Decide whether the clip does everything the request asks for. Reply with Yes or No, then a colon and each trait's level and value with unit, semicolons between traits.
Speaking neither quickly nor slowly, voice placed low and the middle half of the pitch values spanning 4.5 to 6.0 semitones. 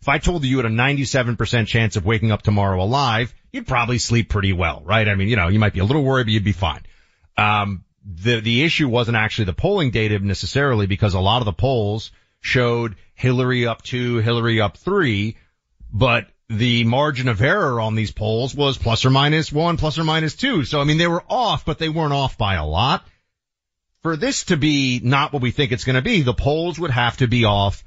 No: fast, 230 wpm; low, 120 Hz; average, 4.8 semitones